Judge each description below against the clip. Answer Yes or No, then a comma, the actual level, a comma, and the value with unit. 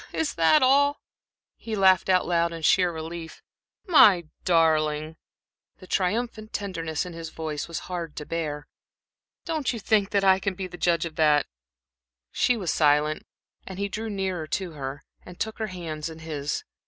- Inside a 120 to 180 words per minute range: Yes, average, 165 wpm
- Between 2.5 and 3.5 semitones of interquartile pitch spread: No, average, 3.9 semitones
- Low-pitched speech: No, medium, 175 Hz